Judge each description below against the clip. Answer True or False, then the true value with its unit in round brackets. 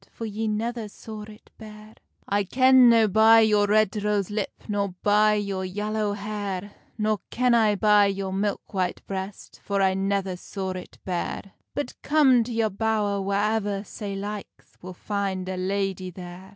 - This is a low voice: False (205 Hz)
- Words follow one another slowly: False (165 wpm)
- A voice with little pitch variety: True (1.9 semitones)